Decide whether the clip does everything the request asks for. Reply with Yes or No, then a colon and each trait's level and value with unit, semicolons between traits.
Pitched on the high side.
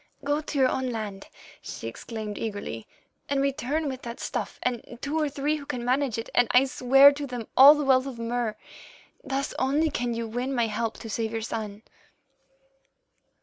Yes: very high, 250 Hz